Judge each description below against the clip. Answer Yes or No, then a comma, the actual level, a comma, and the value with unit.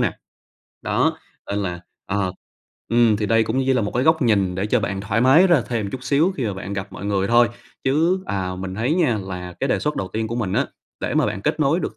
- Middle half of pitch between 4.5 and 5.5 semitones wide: Yes, average, 5.1 semitones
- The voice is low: Yes, low, 110 Hz